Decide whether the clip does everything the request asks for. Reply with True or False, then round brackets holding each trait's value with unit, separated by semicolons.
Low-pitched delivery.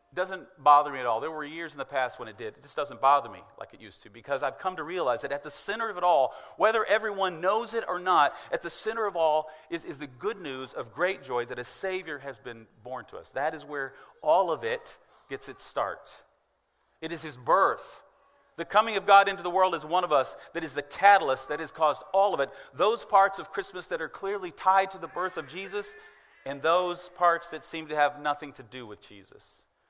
False (170 Hz)